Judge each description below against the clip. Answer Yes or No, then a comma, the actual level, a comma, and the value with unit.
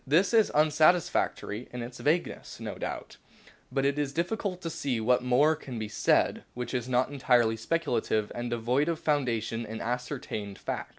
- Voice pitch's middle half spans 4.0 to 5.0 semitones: Yes, average, 4.4 semitones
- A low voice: Yes, low, 125 Hz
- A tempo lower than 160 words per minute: No, average, 170 wpm